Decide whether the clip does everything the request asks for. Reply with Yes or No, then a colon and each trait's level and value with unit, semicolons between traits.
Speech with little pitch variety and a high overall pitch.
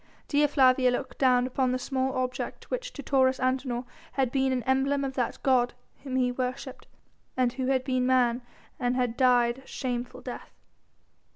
Yes: narrow, 1.1 semitones; very high, 255 Hz